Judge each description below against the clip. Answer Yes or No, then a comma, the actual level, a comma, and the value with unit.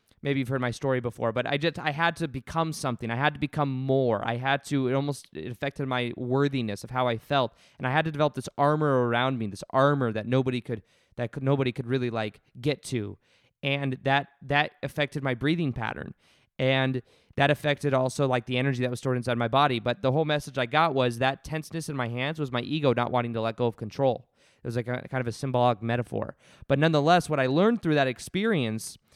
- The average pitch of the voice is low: Yes, low, 130 Hz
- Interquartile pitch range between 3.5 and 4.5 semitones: No, average, 2.8 semitones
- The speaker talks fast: Yes, fast, 235 wpm